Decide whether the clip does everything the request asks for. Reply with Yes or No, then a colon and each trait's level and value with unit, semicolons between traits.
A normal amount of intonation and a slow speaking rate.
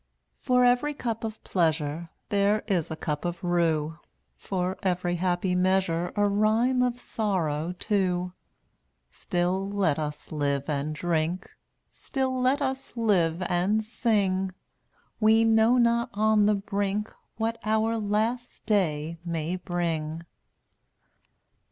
Yes: average, 4.5 semitones; slow, 130 wpm